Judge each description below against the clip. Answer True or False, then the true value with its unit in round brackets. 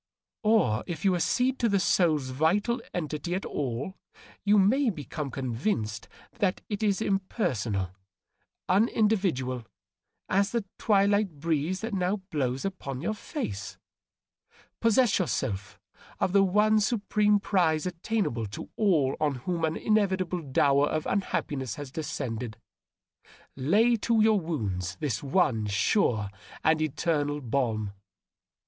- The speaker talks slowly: True (125 wpm)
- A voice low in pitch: False (170 Hz)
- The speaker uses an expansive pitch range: True (7.4 semitones)